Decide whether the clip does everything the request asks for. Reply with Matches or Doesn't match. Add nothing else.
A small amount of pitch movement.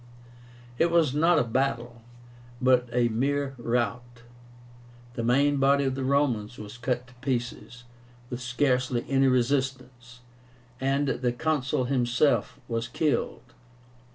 Matches